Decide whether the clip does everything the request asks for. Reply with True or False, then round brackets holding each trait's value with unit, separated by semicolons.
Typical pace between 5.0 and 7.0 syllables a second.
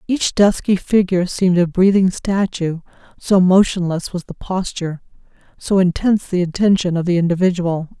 True (5.3 syllables/s)